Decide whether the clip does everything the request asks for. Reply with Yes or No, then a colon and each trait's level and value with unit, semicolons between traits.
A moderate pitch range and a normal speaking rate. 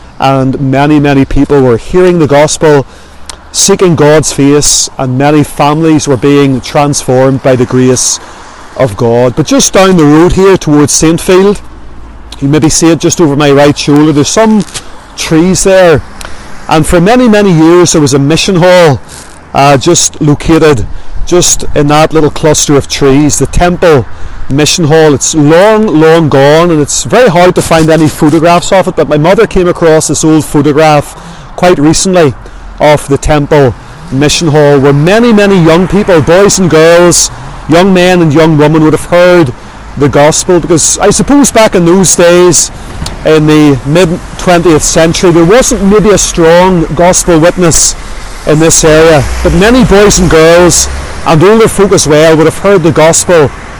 Yes: average, 3.9 semitones; average, 170 wpm